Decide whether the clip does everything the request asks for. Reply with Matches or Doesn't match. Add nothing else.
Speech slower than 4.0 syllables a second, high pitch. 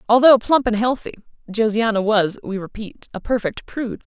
Doesn't match